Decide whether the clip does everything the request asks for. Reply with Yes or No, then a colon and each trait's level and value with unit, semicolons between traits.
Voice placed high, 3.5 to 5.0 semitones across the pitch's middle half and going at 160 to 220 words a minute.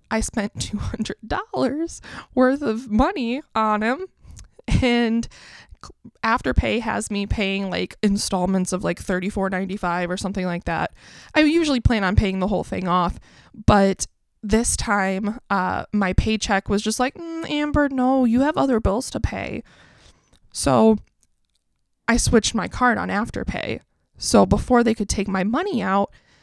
No: high, 215 Hz; average, 4.7 semitones; average, 145 wpm